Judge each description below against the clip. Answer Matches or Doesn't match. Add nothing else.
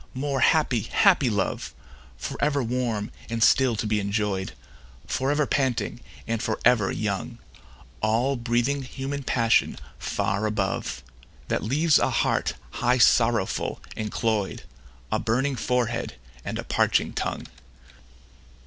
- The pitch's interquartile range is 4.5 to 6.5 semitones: Doesn't match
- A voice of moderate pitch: Doesn't match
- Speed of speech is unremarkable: Doesn't match